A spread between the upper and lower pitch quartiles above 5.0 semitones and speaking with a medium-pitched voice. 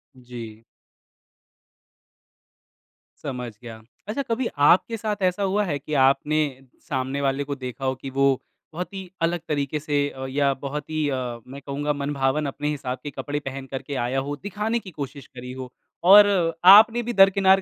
Yes: wide, 5.4 semitones; medium, 145 Hz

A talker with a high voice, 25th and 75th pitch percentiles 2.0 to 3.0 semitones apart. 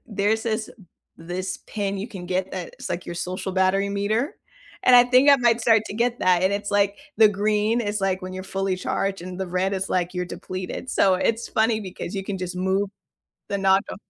Yes: high, 195 Hz; average, 2.7 semitones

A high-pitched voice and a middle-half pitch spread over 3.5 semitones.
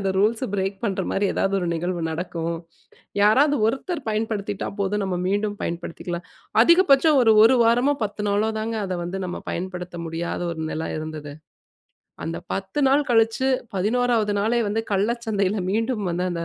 Yes: high, 205 Hz; average, 4.0 semitones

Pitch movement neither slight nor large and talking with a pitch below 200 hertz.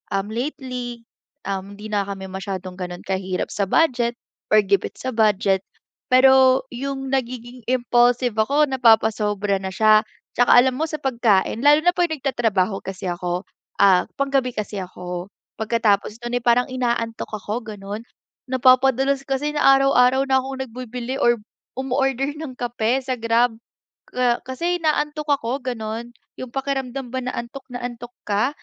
No: average, 4.0 semitones; high, 240 Hz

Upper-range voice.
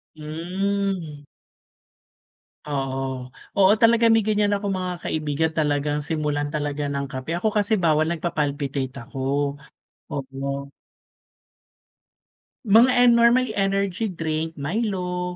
No: medium, 165 Hz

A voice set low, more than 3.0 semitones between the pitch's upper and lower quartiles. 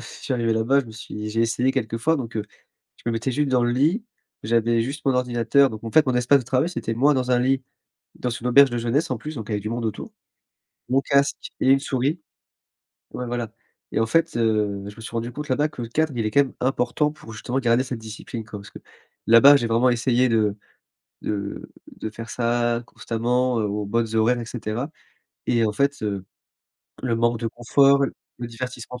No: low, 120 Hz; average, 2.7 semitones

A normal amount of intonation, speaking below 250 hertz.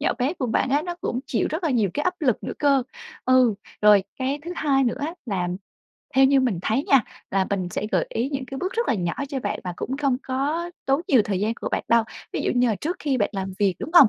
No: average, 4.8 semitones; very high, 260 Hz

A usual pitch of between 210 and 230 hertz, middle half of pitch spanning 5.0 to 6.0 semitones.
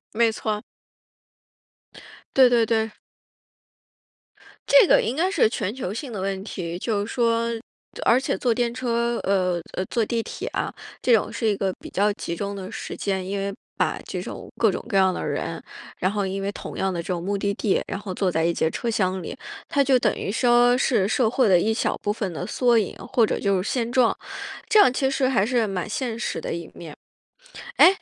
No: high, 215 Hz; average, 3.9 semitones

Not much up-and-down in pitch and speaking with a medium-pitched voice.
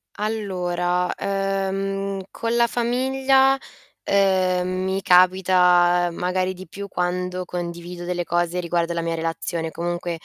Yes: narrow, 2.0 semitones; medium, 180 Hz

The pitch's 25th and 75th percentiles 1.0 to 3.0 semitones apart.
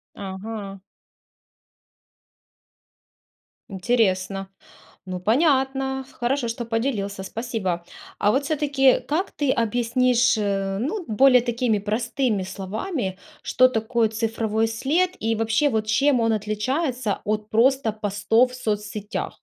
No: average, 3.8 semitones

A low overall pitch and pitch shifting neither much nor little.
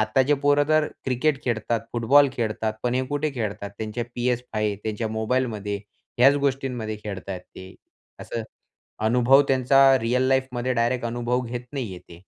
Yes: low, 120 Hz; average, 3.3 semitones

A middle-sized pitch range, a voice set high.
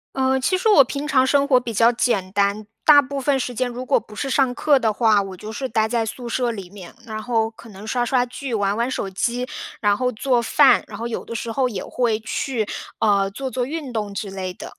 Yes: average, 3.6 semitones; high, 235 Hz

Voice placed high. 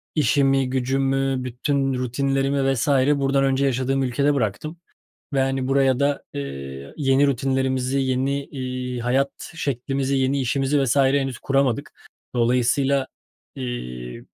No: low, 135 Hz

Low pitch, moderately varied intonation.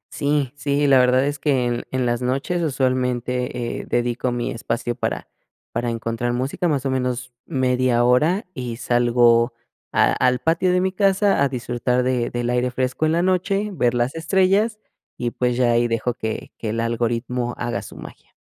Yes: low, 125 Hz; average, 3.0 semitones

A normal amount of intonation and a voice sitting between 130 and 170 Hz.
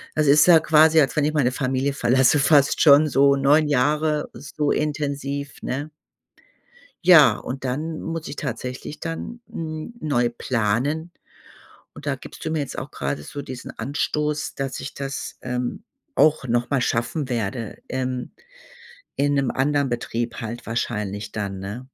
Yes: average, 3.5 semitones; medium, 140 Hz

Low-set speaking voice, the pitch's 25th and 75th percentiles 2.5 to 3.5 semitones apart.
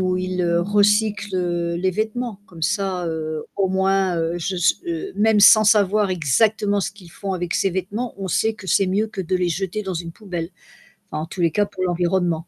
No: high, 190 Hz; average, 2.9 semitones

